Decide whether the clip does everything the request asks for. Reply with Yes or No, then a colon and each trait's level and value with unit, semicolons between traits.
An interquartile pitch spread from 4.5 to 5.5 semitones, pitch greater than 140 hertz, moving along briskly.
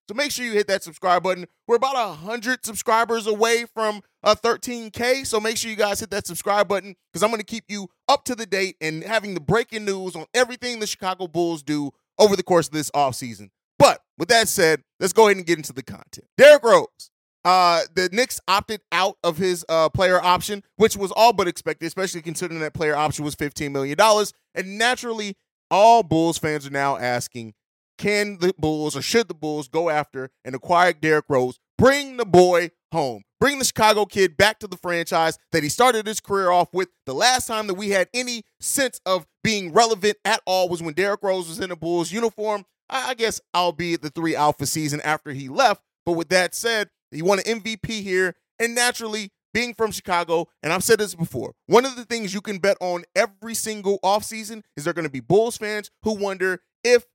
Yes: average, 4.9 semitones; high, 190 Hz; fast, 215 wpm